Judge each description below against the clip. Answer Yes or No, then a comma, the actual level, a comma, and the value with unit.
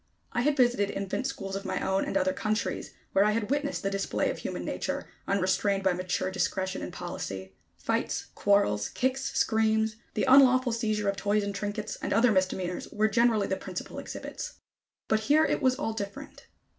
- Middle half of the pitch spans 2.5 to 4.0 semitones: Yes, average, 3.7 semitones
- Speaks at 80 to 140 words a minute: No, average, 180 wpm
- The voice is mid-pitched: No, high, 205 Hz